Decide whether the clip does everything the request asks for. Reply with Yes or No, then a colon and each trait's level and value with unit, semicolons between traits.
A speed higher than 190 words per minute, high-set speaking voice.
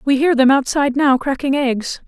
Yes: average, 200 wpm; very high, 270 Hz